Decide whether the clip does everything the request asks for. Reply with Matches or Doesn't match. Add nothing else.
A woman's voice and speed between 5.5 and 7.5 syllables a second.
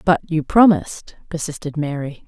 Doesn't match